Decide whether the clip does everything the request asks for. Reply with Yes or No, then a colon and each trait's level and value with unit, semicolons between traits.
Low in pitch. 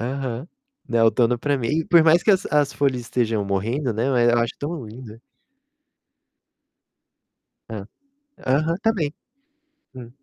Yes: low, 130 Hz